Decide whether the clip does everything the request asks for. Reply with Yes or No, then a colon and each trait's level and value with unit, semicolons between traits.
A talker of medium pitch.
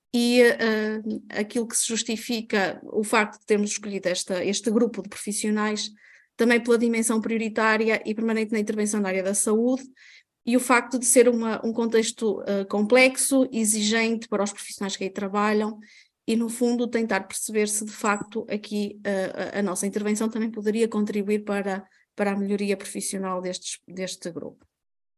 No: high, 215 Hz